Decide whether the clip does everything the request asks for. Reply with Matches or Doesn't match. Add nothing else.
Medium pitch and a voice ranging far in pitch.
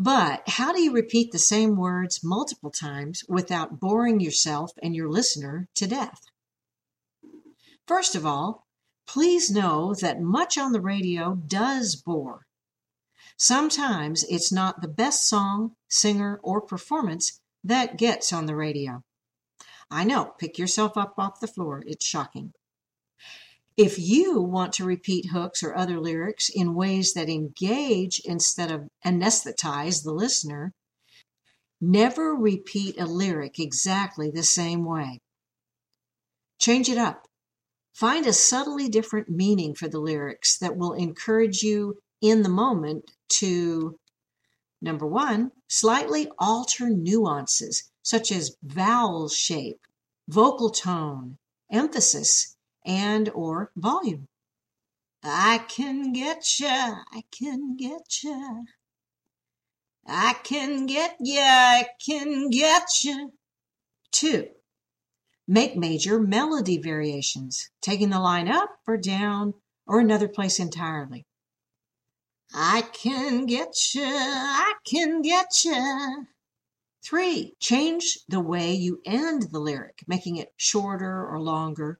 Doesn't match